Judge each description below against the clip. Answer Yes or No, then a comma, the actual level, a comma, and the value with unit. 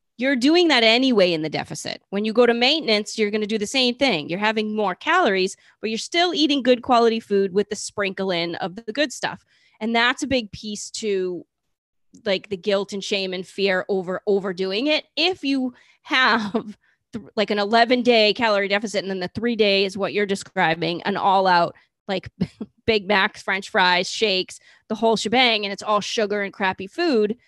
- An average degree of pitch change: Yes, average, 3.3 semitones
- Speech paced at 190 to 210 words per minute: Yes, average, 200 wpm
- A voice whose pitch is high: Yes, high, 210 Hz